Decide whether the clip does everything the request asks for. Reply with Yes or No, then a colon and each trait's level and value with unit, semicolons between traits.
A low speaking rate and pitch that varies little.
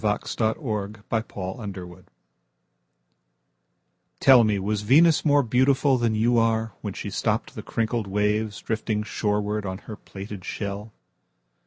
Yes: slow, 105 wpm; narrow, 2.2 semitones